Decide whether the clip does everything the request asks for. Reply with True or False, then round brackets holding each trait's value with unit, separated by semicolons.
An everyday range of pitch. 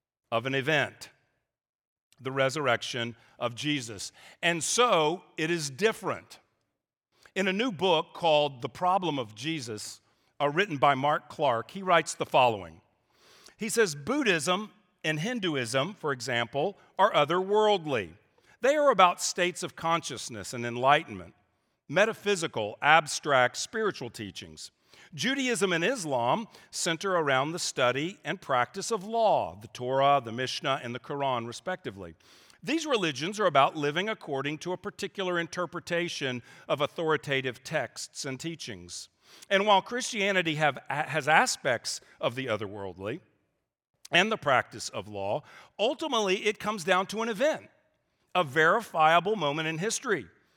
False (6.9 semitones)